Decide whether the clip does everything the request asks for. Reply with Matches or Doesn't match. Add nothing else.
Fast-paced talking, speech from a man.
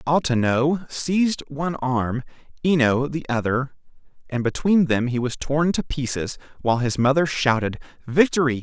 Doesn't match